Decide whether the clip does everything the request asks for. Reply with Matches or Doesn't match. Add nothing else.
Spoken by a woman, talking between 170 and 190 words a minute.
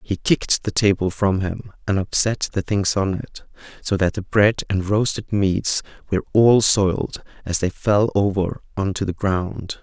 Doesn't match